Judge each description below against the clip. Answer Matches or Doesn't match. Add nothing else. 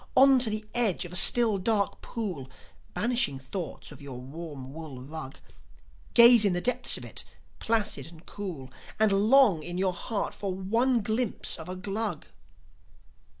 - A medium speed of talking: Matches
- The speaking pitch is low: Doesn't match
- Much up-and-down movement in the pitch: Matches